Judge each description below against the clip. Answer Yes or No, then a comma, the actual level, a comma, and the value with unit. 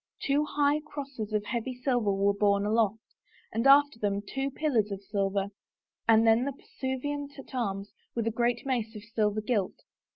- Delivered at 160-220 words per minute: Yes, average, 170 wpm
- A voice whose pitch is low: No, high, 230 Hz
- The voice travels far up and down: No, average, 4.7 semitones